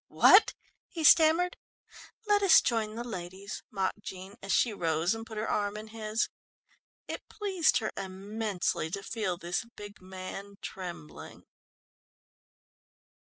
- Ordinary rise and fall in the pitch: Yes, average, 3.3 semitones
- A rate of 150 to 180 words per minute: No, slow, 135 wpm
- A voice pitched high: Yes, high, 210 Hz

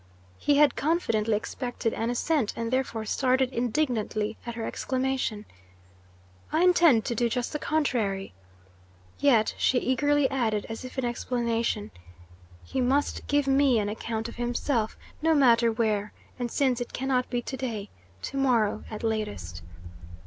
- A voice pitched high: Yes, high, 240 Hz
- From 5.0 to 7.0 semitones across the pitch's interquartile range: No, average, 3.3 semitones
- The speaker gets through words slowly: No, average, 150 wpm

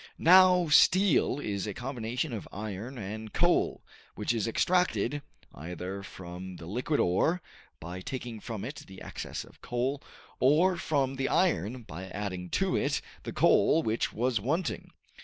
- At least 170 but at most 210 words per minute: No, average, 150 wpm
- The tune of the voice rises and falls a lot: Yes, wide, 6.9 semitones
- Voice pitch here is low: Yes, low, 120 Hz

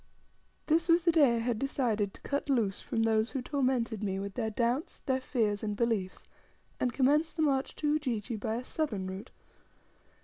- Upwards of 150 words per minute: Yes, average, 190 wpm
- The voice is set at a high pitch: Yes, high, 240 Hz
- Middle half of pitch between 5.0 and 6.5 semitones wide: No, average, 4.6 semitones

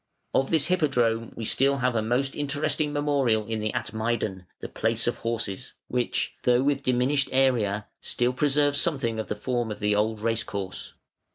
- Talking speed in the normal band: Yes, average, 170 wpm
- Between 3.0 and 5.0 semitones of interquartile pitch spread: Yes, average, 3.9 semitones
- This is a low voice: Yes, low, 120 Hz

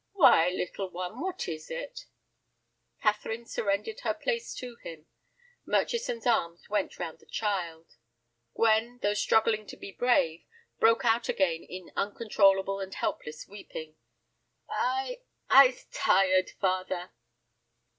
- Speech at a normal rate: No, slow, 115 wpm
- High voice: Yes, high, 205 Hz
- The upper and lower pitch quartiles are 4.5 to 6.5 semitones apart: Yes, average, 4.8 semitones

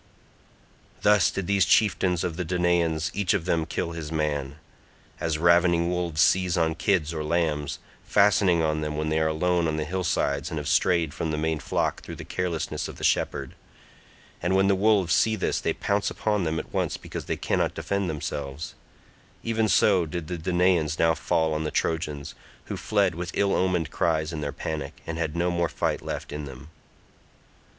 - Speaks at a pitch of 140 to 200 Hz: No, very low, 85 Hz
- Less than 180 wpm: No, average, 185 wpm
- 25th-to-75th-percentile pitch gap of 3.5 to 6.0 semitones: No, average, 2.7 semitones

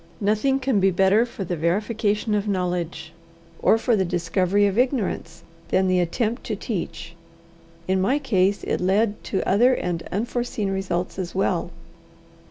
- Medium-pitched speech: No, high, 195 Hz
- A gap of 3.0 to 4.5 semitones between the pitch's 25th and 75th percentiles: Yes, average, 3.5 semitones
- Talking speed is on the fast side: No, average, 155 wpm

